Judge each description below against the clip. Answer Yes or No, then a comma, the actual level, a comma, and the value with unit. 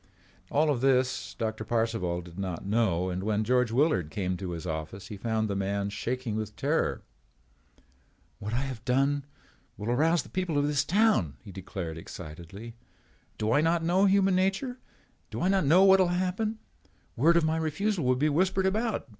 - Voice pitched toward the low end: Yes, low, 125 Hz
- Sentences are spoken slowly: No, average, 180 wpm